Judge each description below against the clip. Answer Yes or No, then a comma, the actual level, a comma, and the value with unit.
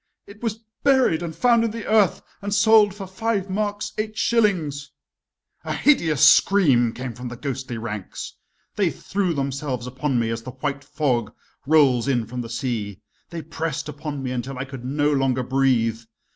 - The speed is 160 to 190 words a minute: Yes, average, 175 wpm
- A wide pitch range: Yes, wide, 7.7 semitones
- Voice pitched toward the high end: No, medium, 140 Hz